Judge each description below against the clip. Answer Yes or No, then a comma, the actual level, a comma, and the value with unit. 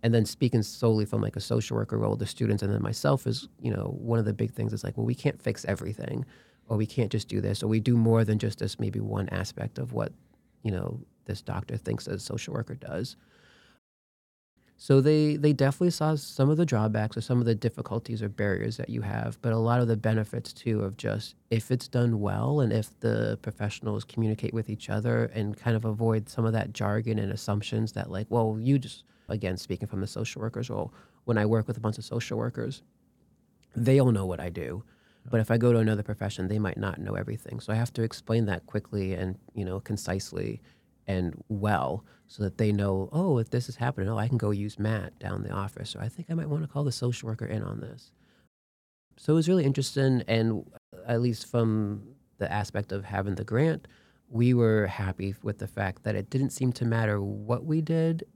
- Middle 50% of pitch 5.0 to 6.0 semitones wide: No, average, 2.8 semitones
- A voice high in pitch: No, low, 115 Hz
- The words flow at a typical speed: No, fast, 225 wpm